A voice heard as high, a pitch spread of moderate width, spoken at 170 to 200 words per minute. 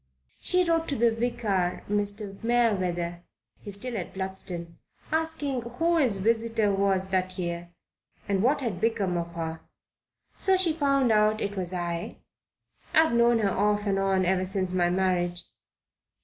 No: high, 200 Hz; average, 4.4 semitones; average, 155 wpm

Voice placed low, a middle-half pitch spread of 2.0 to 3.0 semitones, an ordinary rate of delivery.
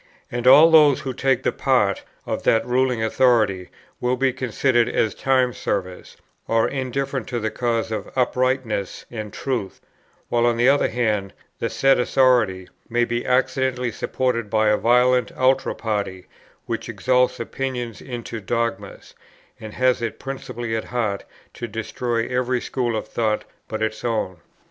Yes: low, 120 Hz; average, 2.7 semitones; average, 155 wpm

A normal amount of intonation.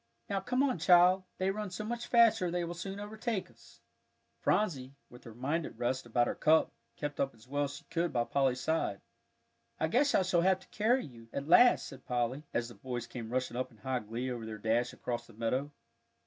No: wide, 7.5 semitones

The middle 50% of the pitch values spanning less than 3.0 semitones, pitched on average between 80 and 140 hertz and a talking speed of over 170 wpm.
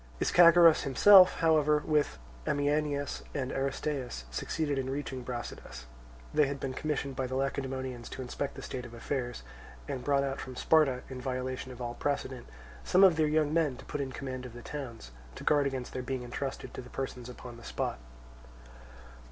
Yes: narrow, 2.6 semitones; low, 135 Hz; average, 180 wpm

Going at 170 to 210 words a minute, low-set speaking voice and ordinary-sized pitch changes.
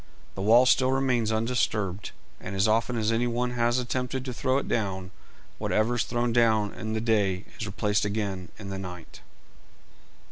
Yes: average, 175 wpm; low, 110 Hz; average, 3.2 semitones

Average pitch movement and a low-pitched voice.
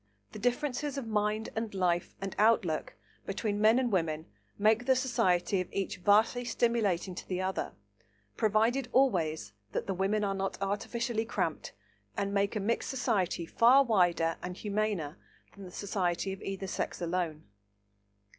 No: average, 4.0 semitones; high, 200 Hz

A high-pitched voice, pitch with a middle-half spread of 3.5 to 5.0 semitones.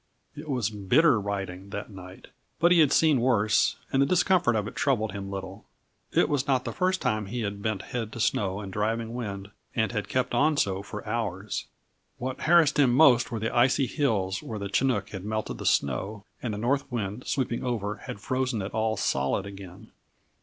No: low, 110 Hz; average, 4.4 semitones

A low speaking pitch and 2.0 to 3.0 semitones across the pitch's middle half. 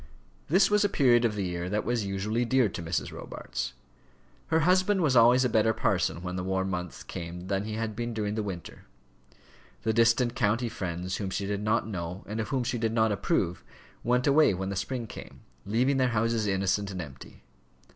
No: low, 110 Hz; average, 4.1 semitones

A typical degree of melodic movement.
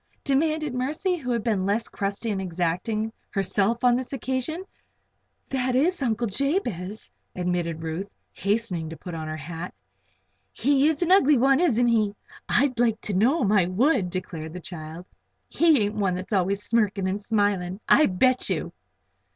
No: wide, 6.0 semitones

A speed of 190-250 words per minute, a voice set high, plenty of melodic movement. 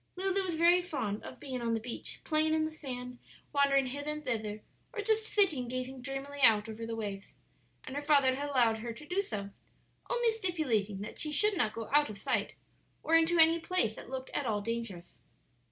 Yes: fast, 205 wpm; very high, 270 Hz; wide, 5.9 semitones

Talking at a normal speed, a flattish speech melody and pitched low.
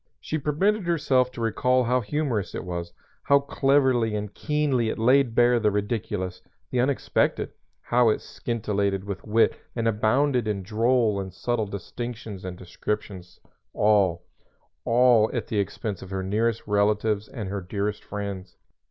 No: average, 150 wpm; average, 3.7 semitones; low, 110 Hz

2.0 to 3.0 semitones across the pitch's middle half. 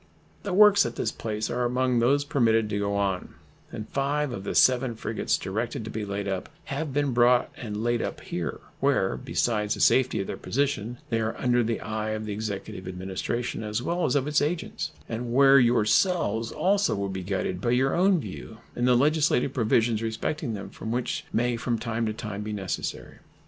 No: average, 3.8 semitones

